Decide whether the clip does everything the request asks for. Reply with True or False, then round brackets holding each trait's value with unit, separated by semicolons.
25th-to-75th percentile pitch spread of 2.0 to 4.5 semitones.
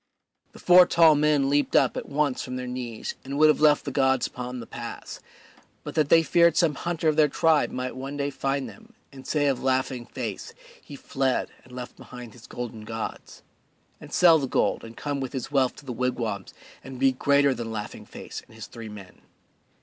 True (3.1 semitones)